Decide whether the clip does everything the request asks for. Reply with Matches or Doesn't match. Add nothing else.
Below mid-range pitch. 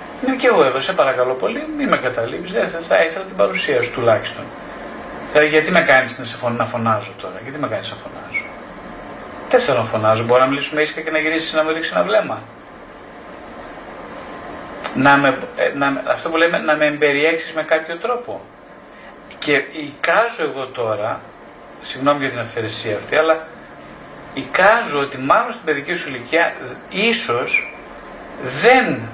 Doesn't match